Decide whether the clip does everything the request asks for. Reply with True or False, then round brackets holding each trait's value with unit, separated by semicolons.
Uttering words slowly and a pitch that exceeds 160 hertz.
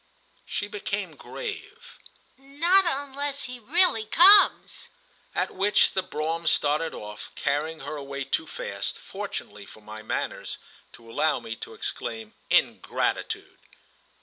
True (120 wpm; 185 Hz)